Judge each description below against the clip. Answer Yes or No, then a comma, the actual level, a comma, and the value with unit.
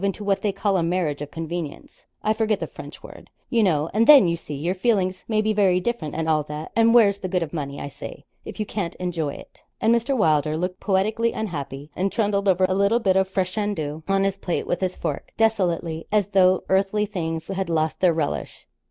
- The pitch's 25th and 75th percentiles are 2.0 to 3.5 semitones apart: No, average, 4.1 semitones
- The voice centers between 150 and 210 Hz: Yes, medium, 185 Hz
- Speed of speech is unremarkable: No, fast, 220 wpm